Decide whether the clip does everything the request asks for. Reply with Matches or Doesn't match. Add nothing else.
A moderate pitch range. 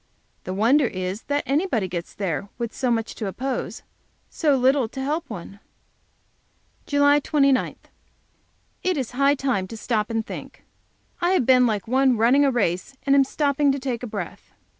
Matches